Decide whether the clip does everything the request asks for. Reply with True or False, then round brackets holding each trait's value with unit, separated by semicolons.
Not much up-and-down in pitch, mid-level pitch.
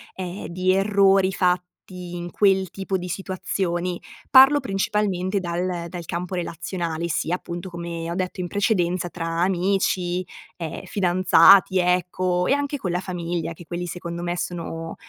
True (1.6 semitones; 180 Hz)